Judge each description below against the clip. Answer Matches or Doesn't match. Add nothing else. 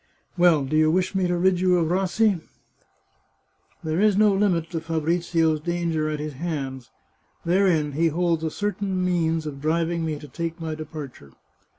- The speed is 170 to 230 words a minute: Matches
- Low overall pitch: Doesn't match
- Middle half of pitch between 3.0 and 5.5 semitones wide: Doesn't match